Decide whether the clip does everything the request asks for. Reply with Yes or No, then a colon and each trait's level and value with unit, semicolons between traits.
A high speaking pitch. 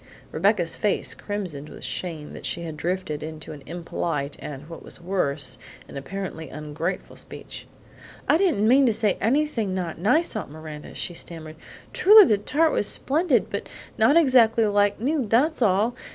Yes: high, 195 Hz